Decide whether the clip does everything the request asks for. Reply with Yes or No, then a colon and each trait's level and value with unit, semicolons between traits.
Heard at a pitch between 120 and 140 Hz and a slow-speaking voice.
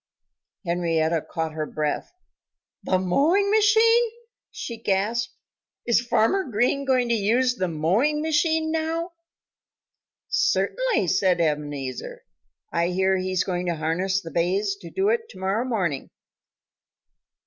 No: high, 195 Hz; slow, 125 wpm